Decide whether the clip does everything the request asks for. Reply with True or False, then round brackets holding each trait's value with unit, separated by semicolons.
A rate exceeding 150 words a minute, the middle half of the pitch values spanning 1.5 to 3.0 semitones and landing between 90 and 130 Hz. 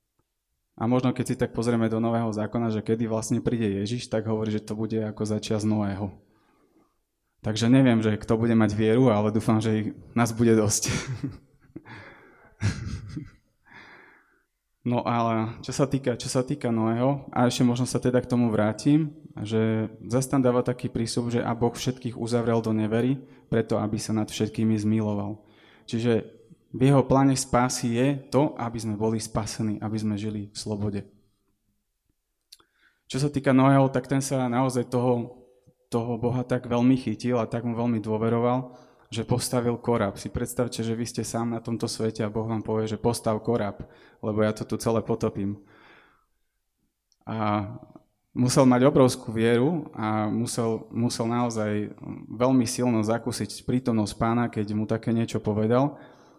True (160 wpm; 2.4 semitones; 115 Hz)